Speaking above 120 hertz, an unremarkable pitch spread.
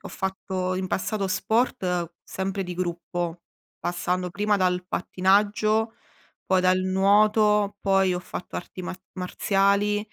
No: high, 190 Hz; narrow, 2.1 semitones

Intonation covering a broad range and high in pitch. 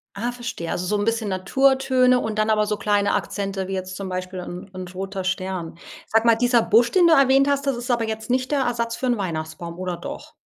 No: average, 4.7 semitones; high, 215 Hz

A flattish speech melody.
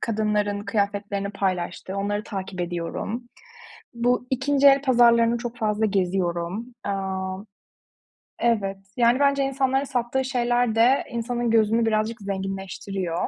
No: average, 3.6 semitones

